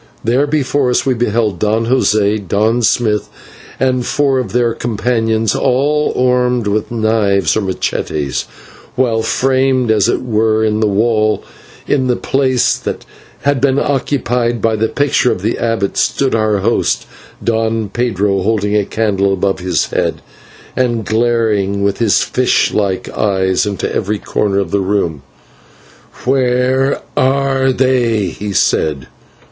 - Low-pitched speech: Yes, low, 115 Hz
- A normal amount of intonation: Yes, average, 3.6 semitones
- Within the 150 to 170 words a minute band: No, average, 140 wpm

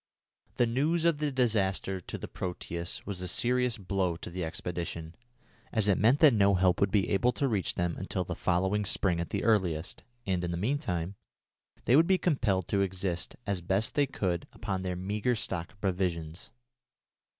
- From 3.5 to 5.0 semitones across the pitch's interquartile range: Yes, average, 4.5 semitones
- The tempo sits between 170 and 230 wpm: Yes, average, 185 wpm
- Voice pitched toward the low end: Yes, very low, 95 Hz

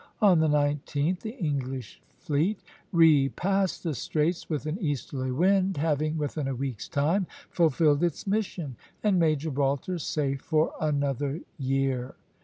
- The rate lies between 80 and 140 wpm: Yes, slow, 135 wpm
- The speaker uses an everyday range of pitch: Yes, average, 3.7 semitones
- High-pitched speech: No, medium, 150 Hz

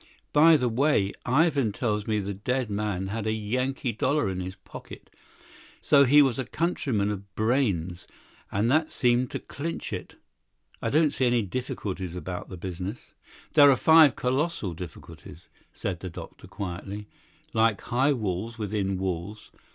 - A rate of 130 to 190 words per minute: Yes, average, 155 wpm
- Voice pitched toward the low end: Yes, low, 110 Hz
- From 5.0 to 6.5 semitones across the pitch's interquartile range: Yes, wide, 5.5 semitones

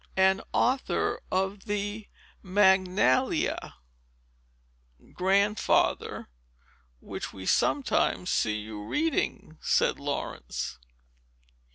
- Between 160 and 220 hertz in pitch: Yes, high, 190 Hz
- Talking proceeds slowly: Yes, slow, 70 wpm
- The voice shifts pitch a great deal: Yes, wide, 6.2 semitones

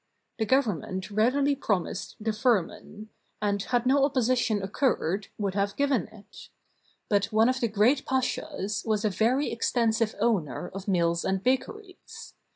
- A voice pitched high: Yes, high, 220 Hz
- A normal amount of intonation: Yes, average, 4.2 semitones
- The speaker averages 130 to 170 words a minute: Yes, average, 145 wpm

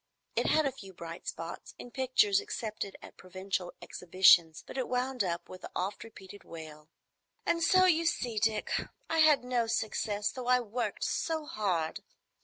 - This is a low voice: No, high, 215 Hz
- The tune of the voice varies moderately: No, wide, 6.1 semitones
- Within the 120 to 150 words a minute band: No, average, 170 wpm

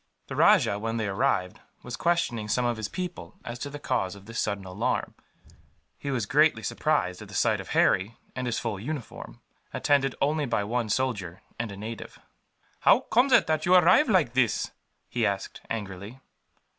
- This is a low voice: Yes, low, 120 Hz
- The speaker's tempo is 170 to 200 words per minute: Yes, average, 180 wpm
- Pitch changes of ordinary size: No, wide, 5.9 semitones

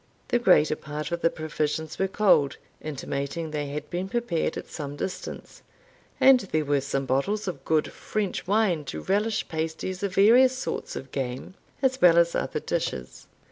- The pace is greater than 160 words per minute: Yes, average, 170 wpm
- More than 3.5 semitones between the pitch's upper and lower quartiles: Yes, average, 5.2 semitones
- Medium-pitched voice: Yes, medium, 165 Hz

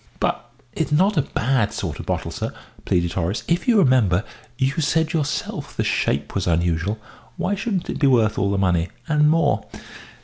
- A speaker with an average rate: Yes, average, 180 wpm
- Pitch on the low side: Yes, low, 130 Hz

